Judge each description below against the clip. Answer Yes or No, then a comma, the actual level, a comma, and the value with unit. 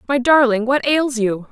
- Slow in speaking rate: No, average, 200 wpm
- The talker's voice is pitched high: Yes, very high, 255 Hz